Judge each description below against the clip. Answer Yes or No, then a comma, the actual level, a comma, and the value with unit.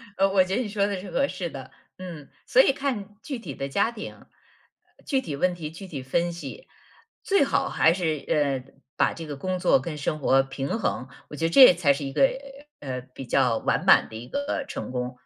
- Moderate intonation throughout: No, wide, 6.7 semitones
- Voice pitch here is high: No, medium, 170 Hz